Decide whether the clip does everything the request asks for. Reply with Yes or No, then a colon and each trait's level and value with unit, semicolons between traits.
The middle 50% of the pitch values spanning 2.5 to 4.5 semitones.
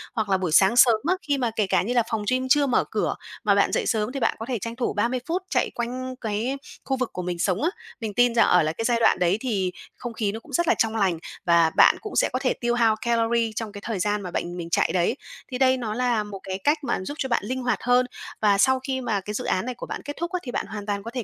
Yes: average, 3.8 semitones